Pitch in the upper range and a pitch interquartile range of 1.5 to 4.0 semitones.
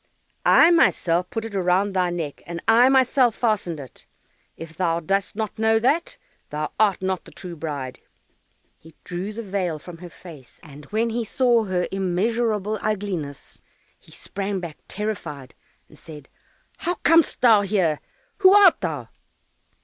No: high, 195 Hz; average, 4.9 semitones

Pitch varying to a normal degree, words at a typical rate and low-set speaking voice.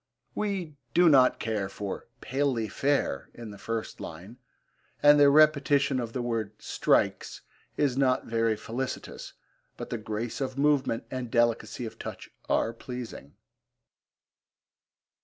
No: average, 3.7 semitones; slow, 130 wpm; low, 125 Hz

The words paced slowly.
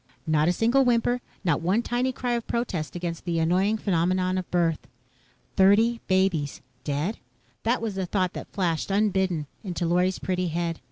No: average, 165 wpm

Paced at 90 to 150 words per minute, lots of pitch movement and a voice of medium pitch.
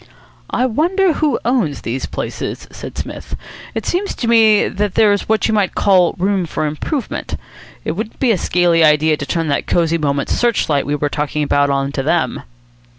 No: average, 190 wpm; wide, 7.1 semitones; medium, 175 Hz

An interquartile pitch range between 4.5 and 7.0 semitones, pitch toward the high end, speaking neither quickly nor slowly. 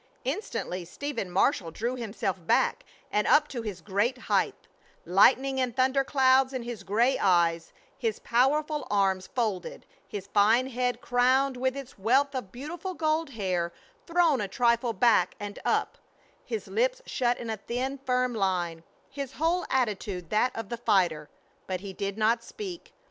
Yes: average, 5.2 semitones; high, 240 Hz; average, 160 wpm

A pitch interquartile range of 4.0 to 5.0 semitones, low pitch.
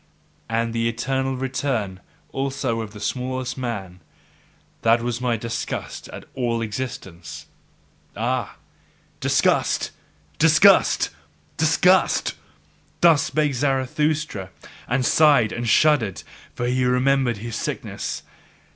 No: average, 2.8 semitones; low, 125 Hz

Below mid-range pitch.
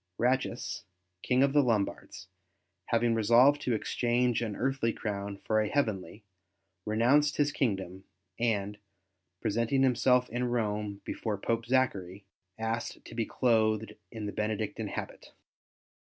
Yes: low, 115 Hz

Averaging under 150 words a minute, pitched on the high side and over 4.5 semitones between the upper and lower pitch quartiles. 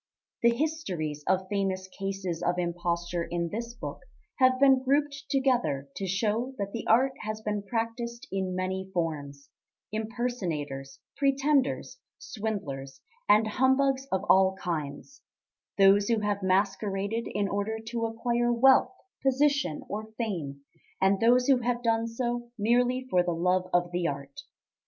Yes: average, 140 wpm; high, 210 Hz; average, 5.1 semitones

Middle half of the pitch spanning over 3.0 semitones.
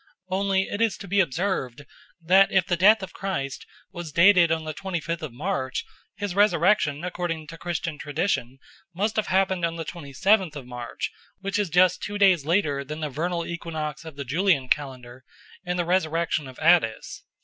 Yes: average, 4.3 semitones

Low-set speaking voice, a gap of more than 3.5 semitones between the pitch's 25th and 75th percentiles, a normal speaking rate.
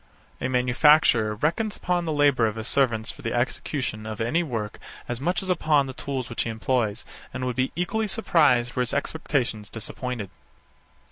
Yes: low, 130 Hz; average, 4.7 semitones; average, 180 wpm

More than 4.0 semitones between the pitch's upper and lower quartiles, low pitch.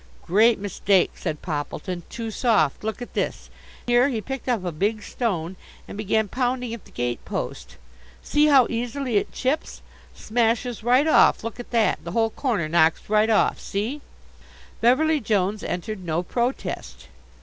No: average, 4.4 semitones; high, 220 Hz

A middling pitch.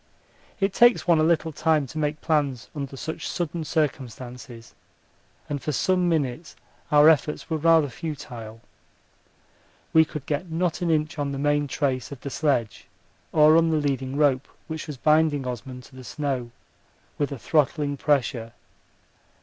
Yes: medium, 145 Hz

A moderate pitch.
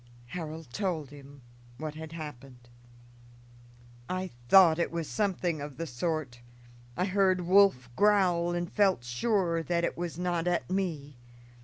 Yes: medium, 170 Hz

